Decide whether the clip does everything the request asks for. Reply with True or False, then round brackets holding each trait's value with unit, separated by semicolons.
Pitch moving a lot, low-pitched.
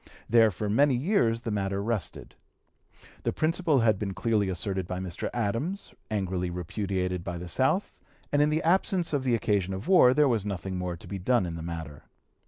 True (5.9 semitones; 105 Hz)